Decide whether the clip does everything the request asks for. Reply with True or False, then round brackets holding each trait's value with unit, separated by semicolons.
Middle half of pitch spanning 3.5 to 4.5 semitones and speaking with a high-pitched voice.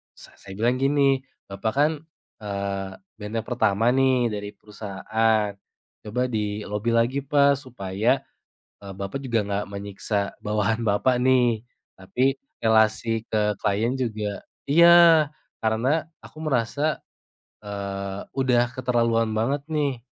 False (4.1 semitones; 115 Hz)